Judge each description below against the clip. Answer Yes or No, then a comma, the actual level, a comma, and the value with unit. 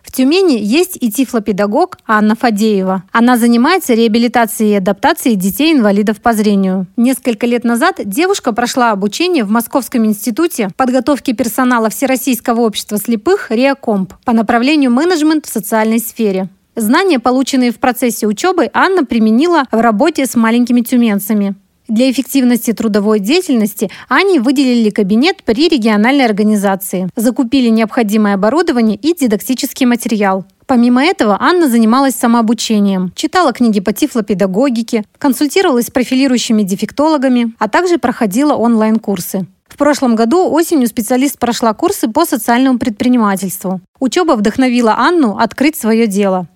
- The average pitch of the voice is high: Yes, high, 240 Hz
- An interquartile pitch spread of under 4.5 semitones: Yes, average, 4.0 semitones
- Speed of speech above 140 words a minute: No, average, 125 wpm